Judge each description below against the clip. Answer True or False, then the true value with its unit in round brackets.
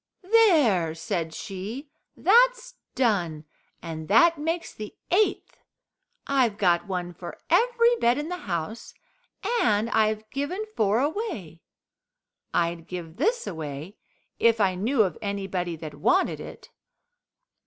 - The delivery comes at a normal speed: False (120 wpm)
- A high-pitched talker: True (215 Hz)